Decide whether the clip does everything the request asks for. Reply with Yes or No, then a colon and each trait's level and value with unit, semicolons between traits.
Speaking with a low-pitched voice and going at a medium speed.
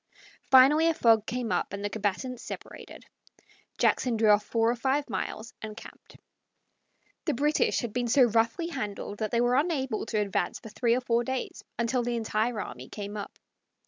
No: high, 235 Hz; average, 180 wpm